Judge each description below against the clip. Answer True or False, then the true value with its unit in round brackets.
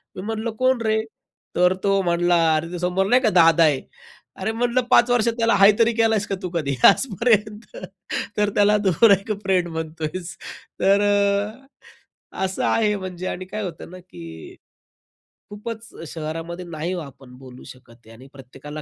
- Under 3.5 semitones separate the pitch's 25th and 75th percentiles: False (5.0 semitones)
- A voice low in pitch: False (185 Hz)